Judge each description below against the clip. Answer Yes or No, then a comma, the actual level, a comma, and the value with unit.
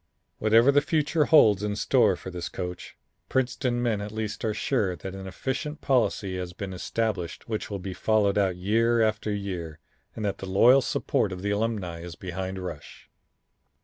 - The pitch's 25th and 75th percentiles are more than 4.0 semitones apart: No, average, 3.6 semitones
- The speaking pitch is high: No, low, 105 Hz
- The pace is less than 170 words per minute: No, average, 180 wpm